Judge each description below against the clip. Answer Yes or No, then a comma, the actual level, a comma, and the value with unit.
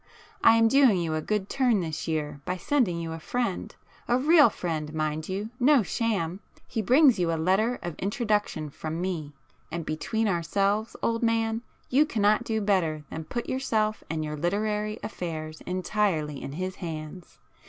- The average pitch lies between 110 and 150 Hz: No, high, 190 Hz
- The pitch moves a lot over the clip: Yes, wide, 5.8 semitones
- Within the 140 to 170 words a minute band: Yes, average, 165 wpm